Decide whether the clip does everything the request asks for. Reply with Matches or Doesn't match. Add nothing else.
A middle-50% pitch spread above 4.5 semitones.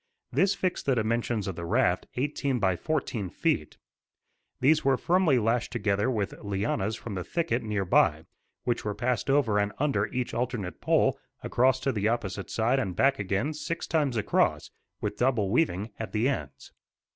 Matches